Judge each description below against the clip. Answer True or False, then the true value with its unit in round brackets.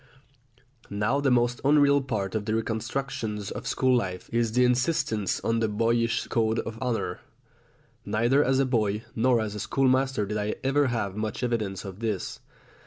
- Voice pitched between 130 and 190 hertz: False (115 Hz)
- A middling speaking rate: True (170 wpm)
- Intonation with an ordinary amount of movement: True (3.3 semitones)